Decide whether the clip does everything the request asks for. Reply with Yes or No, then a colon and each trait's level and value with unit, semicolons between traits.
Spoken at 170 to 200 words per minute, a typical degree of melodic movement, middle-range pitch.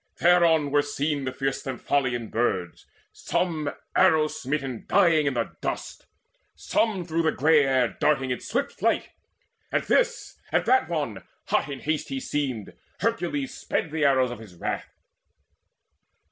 No: average, 145 wpm; average, 3.8 semitones; medium, 145 Hz